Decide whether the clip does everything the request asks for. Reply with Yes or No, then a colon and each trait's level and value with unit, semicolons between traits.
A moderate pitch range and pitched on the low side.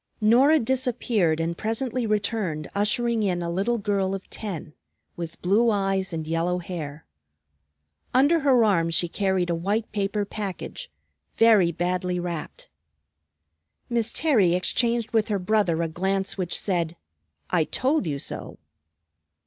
No: average, 4.6 semitones; high, 195 Hz